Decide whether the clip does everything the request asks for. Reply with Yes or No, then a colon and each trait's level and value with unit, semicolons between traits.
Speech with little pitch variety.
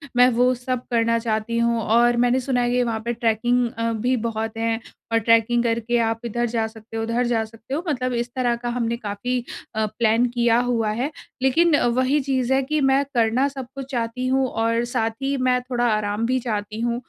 Yes: narrow, 1.9 semitones